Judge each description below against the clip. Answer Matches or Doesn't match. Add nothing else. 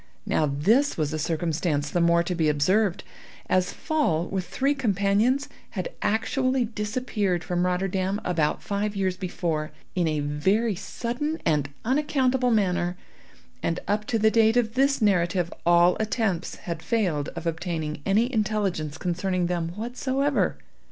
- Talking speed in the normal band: Matches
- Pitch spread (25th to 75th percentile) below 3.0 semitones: Doesn't match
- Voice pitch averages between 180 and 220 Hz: Matches